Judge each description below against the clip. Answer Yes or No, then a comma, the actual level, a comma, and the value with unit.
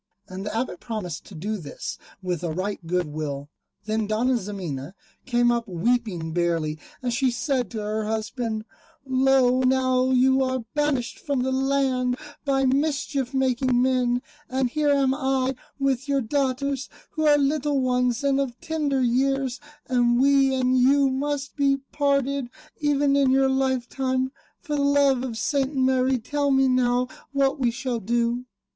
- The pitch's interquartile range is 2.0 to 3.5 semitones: Yes, narrow, 2.6 semitones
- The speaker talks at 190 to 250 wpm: No, average, 160 wpm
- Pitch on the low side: No, very high, 260 Hz